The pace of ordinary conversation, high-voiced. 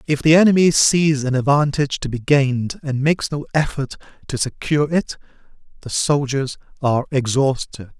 No: average, 150 wpm; medium, 140 Hz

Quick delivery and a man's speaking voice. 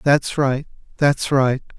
No: slow, 135 wpm; male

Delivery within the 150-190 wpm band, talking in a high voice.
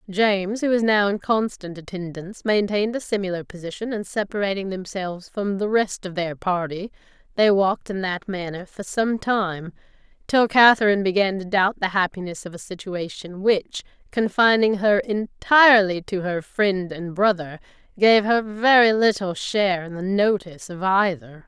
Yes: average, 160 wpm; high, 195 Hz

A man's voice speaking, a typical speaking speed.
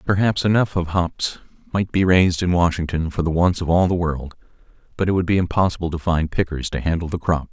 No: male; fast, 225 wpm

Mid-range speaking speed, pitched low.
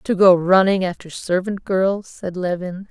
No: average, 165 wpm; medium, 185 Hz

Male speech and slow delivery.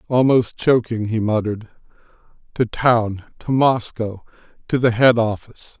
Yes: male; slow, 105 wpm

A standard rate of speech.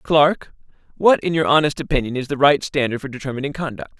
Yes: average, 195 wpm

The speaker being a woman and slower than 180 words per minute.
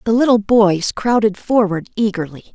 Yes: female; average, 140 wpm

